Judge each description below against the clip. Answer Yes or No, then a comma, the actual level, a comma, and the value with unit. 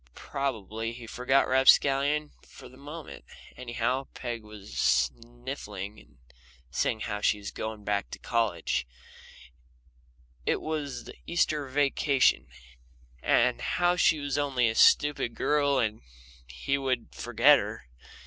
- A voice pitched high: No, low, 125 Hz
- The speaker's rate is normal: No, slow, 125 wpm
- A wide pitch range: No, average, 4.6 semitones